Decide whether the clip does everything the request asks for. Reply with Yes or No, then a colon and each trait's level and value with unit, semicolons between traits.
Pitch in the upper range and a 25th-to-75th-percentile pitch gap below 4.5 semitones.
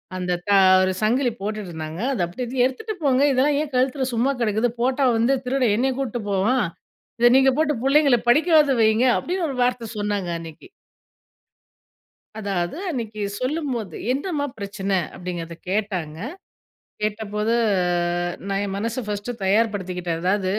No: high, 225 Hz; average, 5.1 semitones